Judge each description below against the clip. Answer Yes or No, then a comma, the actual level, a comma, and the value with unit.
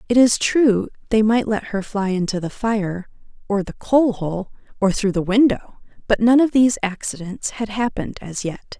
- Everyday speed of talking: Yes, average, 190 wpm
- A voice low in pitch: No, high, 210 Hz